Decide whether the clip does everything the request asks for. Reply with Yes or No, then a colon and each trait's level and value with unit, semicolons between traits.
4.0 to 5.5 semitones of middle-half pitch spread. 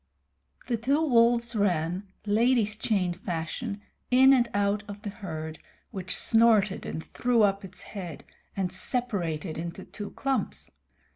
Yes: average, 4.4 semitones